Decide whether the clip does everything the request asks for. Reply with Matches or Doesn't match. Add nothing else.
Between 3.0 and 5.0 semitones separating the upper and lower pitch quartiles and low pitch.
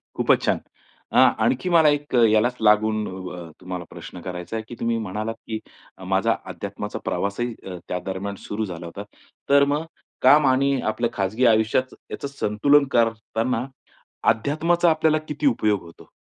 Doesn't match